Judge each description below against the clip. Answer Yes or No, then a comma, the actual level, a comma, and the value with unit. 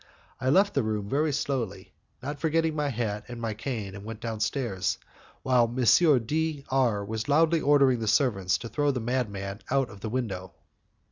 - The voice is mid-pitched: No, low, 120 Hz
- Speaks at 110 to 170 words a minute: No, average, 180 wpm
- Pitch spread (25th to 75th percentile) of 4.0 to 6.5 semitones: Yes, average, 5.1 semitones